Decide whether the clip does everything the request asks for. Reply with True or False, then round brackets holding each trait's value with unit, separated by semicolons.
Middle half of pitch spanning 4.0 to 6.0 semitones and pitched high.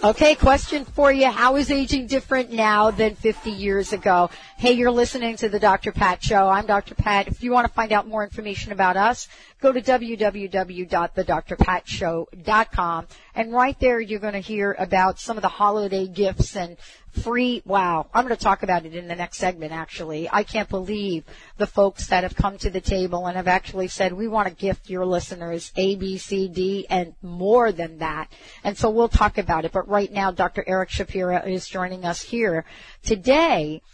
False (3.4 semitones; 200 Hz)